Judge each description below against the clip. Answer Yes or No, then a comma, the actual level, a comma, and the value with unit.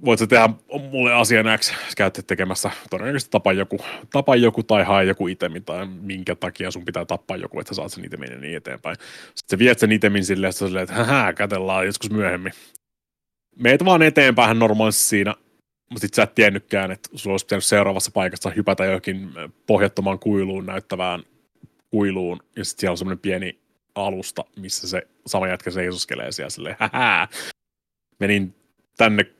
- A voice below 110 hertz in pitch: Yes, low, 100 Hz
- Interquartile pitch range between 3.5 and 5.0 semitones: No, average, 2.7 semitones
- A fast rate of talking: Yes, fast, 165 wpm